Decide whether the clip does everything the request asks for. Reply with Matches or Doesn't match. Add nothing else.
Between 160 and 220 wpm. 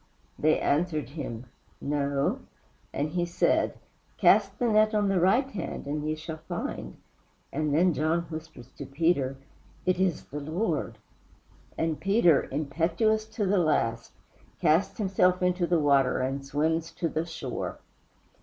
Doesn't match